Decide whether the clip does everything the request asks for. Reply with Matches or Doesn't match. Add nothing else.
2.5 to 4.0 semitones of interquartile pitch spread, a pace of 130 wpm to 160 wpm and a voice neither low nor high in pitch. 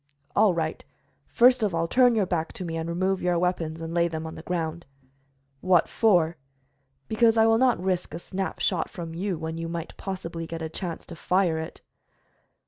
Doesn't match